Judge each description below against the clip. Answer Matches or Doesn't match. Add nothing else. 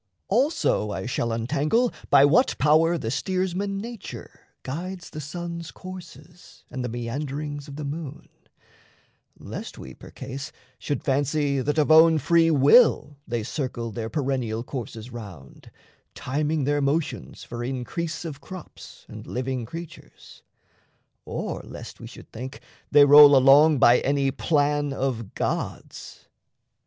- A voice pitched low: Doesn't match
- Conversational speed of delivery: Doesn't match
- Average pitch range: Matches